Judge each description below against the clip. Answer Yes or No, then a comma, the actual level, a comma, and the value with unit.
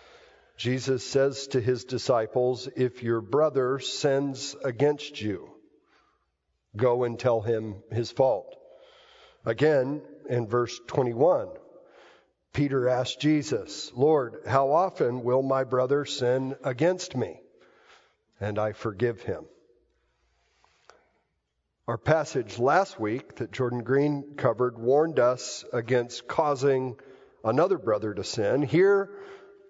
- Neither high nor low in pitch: No, low, 130 Hz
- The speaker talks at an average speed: No, slow, 110 wpm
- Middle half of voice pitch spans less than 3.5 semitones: Yes, average, 2.9 semitones